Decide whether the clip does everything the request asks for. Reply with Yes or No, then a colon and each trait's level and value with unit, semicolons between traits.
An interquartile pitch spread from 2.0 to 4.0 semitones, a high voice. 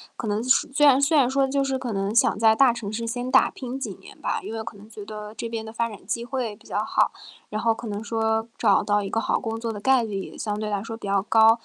Yes: average, 2.7 semitones; high, 225 Hz